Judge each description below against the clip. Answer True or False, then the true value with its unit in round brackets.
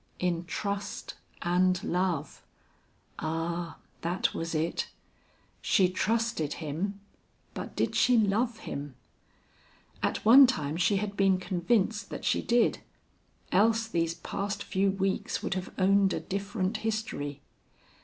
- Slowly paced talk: True (125 wpm)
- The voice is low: False (190 Hz)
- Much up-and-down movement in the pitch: False (3.6 semitones)